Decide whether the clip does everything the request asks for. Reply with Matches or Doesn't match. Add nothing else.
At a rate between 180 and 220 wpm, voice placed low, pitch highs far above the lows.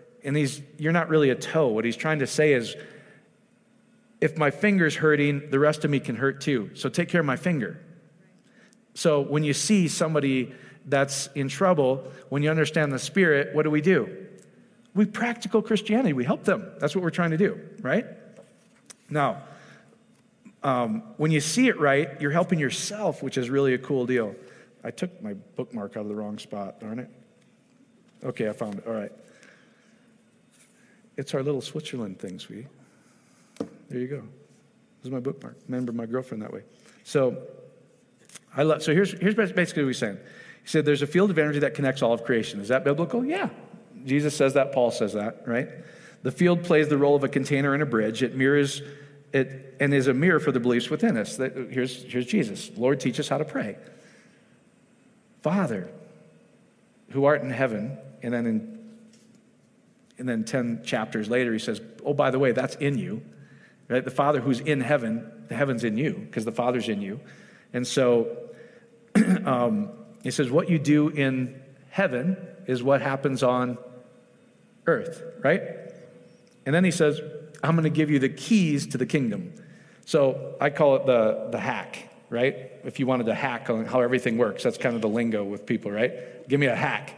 Doesn't match